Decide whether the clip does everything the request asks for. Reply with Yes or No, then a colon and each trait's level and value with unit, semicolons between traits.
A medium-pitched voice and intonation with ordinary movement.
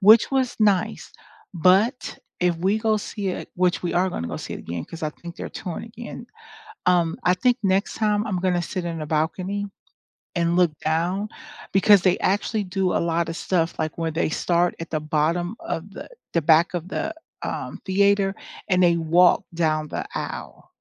Yes: medium, 180 Hz; average, 3.1 semitones